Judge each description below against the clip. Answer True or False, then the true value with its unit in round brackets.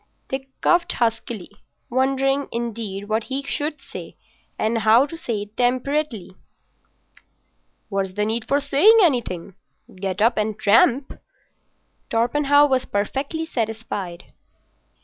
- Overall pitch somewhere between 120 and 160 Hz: False (235 Hz)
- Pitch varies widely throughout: False (4.7 semitones)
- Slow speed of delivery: True (115 wpm)